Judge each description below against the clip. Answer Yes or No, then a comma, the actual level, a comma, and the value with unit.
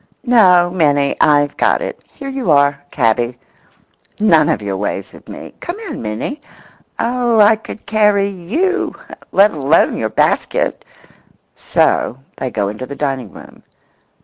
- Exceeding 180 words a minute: No, average, 140 wpm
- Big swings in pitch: Yes, wide, 8.5 semitones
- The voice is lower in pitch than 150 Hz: No, medium, 165 Hz